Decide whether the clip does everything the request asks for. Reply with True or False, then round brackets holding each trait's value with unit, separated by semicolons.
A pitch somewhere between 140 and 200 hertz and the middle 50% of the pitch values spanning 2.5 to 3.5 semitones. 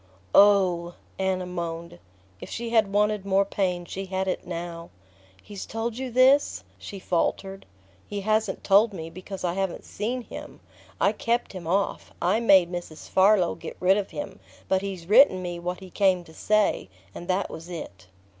True (190 Hz; 2.9 semitones)